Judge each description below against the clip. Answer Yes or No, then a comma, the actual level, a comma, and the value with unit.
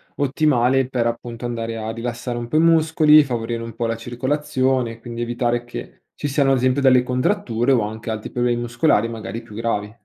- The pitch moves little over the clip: Yes, narrow, 2.3 semitones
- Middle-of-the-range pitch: No, low, 120 Hz